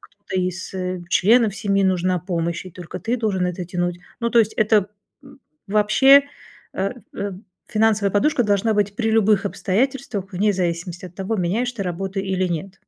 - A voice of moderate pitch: No, high, 195 Hz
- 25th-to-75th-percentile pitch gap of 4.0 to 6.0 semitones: No, average, 3.1 semitones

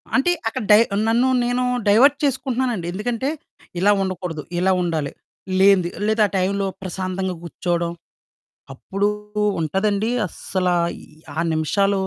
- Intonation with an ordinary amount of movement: Yes, average, 3.9 semitones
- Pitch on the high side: Yes, high, 195 Hz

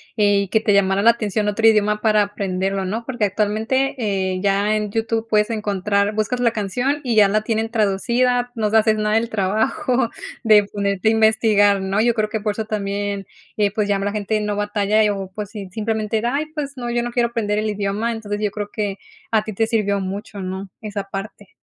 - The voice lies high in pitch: Yes, high, 210 Hz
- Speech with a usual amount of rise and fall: No, narrow, 1.9 semitones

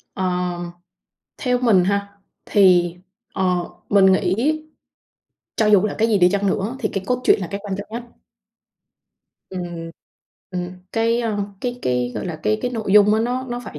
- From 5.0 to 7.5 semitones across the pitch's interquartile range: No, average, 3.9 semitones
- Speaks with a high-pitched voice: Yes, high, 200 Hz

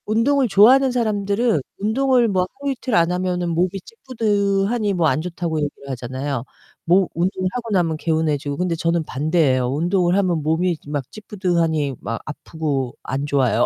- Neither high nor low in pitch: Yes, medium, 175 Hz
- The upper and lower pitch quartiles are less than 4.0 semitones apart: No, average, 5.2 semitones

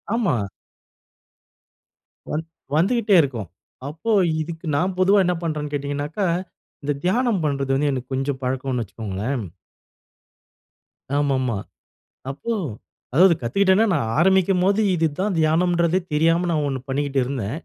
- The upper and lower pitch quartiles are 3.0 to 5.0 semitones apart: No, wide, 5.4 semitones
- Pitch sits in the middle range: Yes, medium, 155 Hz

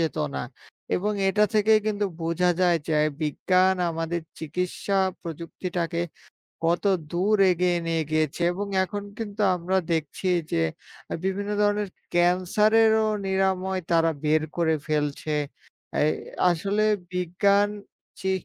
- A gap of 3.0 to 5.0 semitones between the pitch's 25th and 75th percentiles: Yes, average, 3.5 semitones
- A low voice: No, medium, 180 Hz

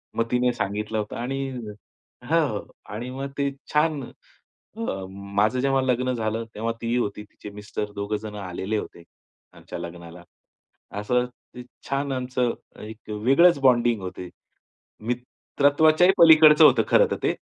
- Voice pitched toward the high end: No, low, 120 Hz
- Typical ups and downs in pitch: Yes, average, 4.5 semitones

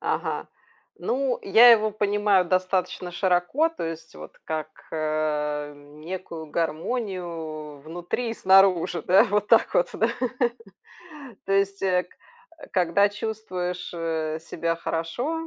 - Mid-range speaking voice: Yes, medium, 180 Hz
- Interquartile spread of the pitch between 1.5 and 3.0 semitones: No, average, 4.2 semitones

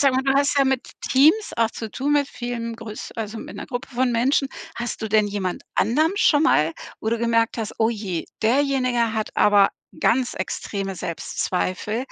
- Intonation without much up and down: No, average, 3.8 semitones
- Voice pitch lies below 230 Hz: No, high, 235 Hz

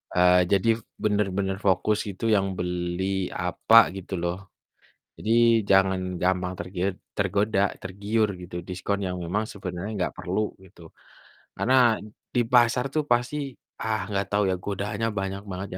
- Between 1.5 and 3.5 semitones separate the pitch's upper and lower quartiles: Yes, average, 2.9 semitones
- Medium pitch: No, low, 100 Hz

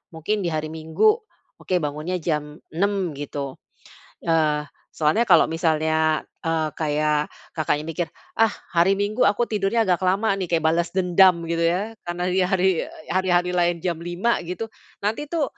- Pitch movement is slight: No, average, 3.3 semitones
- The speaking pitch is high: No, medium, 175 Hz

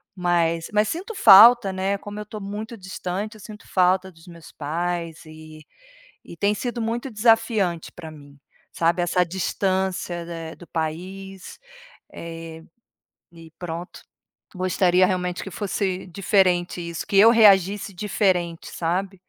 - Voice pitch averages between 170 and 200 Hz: Yes, medium, 185 Hz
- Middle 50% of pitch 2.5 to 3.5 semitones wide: Yes, average, 3.1 semitones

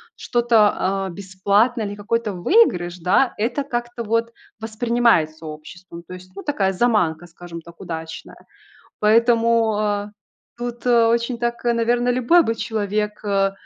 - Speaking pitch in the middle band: No, high, 215 Hz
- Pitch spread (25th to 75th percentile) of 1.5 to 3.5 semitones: No, average, 4.0 semitones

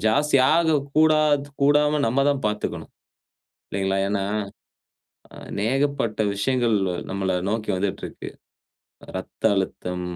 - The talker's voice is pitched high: No, low, 125 Hz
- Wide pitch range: Yes, wide, 6.5 semitones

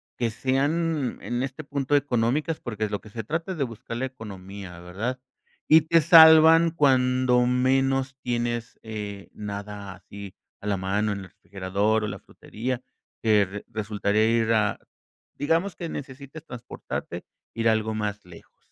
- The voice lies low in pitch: Yes, low, 120 Hz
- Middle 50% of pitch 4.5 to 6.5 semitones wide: Yes, average, 4.8 semitones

